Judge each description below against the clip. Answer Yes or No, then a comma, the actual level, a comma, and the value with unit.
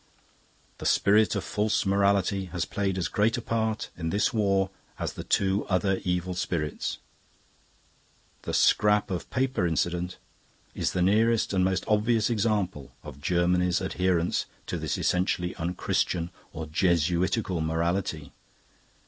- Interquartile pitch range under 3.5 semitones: Yes, average, 2.9 semitones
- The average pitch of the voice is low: Yes, very low, 95 Hz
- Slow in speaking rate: Yes, slow, 130 wpm